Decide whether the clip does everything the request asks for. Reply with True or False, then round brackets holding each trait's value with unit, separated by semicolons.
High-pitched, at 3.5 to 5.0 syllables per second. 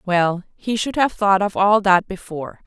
True (195 Hz; 4.6 syllables/s)